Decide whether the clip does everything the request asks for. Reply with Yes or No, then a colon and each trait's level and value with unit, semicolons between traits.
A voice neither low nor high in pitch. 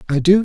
Yes: medium, 175 Hz